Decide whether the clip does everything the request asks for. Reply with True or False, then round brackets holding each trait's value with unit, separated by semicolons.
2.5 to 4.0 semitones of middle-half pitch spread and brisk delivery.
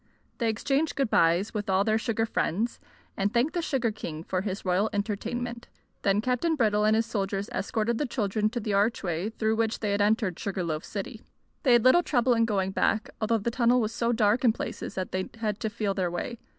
True (2.9 semitones; 215 wpm)